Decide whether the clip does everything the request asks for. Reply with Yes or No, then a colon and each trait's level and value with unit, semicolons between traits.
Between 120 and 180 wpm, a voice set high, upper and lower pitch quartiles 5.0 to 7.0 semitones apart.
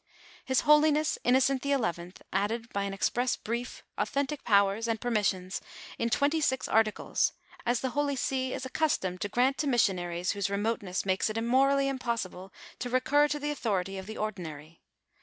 Yes: average, 165 wpm; high, 235 Hz; wide, 5.4 semitones